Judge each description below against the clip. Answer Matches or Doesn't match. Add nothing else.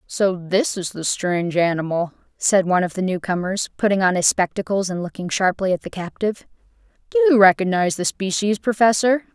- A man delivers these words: Doesn't match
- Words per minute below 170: Doesn't match